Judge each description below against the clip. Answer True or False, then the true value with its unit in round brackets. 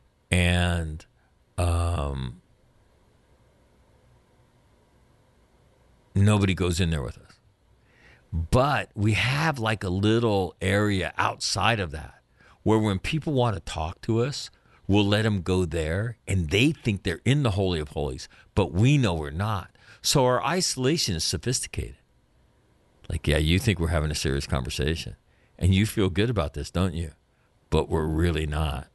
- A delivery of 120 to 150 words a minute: True (145 wpm)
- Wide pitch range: True (5.7 semitones)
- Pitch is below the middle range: True (95 Hz)